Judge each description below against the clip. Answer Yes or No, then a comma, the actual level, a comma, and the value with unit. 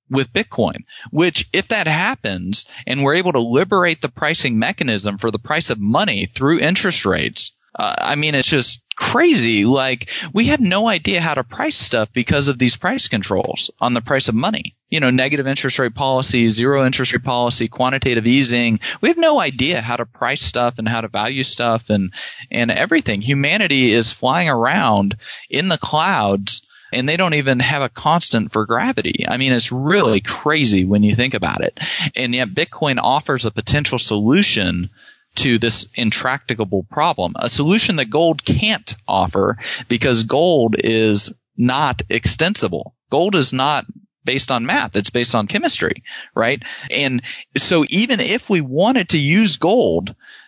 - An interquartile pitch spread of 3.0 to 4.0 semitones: No, average, 5.0 semitones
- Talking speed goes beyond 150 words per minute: Yes, average, 170 wpm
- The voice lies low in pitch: Yes, low, 130 Hz